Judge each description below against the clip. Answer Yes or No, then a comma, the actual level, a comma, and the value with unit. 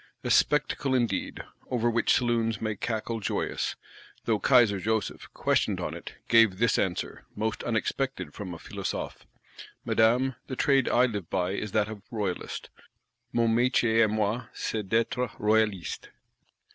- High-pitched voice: No, low, 115 Hz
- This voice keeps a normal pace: Yes, average, 145 wpm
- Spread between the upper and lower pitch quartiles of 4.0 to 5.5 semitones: No, narrow, 2.4 semitones